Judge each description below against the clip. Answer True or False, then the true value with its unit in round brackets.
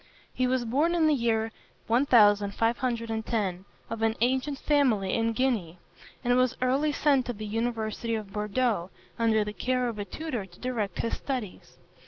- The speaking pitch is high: True (230 Hz)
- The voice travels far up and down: False (3.2 semitones)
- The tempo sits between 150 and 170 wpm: True (160 wpm)